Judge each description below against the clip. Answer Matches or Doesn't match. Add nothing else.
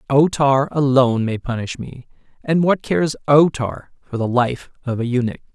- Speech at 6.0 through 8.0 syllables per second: Doesn't match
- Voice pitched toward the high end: Doesn't match